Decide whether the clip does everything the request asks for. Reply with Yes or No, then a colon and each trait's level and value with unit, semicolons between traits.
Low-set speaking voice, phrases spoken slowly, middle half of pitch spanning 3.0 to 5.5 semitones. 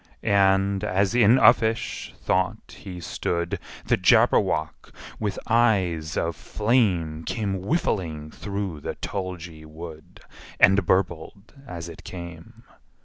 Yes: very low, 95 Hz; slow, 110 wpm; average, 3.5 semitones